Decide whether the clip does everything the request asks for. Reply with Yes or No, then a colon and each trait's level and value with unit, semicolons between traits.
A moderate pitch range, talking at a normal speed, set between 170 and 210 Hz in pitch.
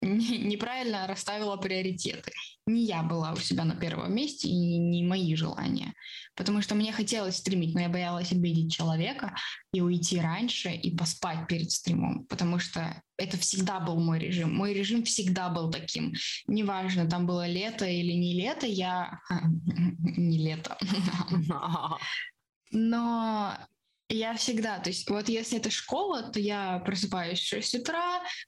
Yes: average, 3.9 semitones; average, 145 wpm; medium, 185 Hz